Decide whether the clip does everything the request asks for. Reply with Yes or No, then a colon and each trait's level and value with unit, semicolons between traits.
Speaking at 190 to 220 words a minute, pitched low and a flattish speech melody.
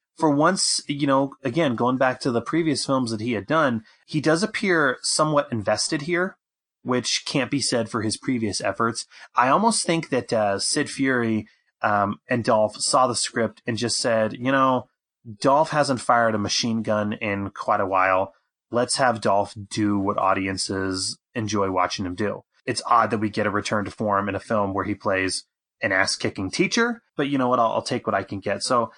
No: average, 200 wpm; low, 115 Hz; average, 5.2 semitones